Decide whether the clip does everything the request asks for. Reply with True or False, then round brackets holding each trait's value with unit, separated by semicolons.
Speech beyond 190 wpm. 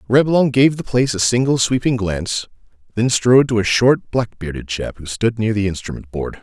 True (205 wpm)